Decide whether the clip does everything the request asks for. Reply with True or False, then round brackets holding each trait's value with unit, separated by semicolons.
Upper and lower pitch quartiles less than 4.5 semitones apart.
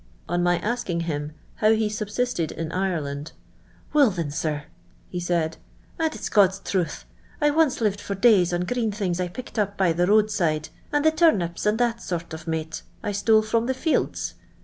False (5.0 semitones)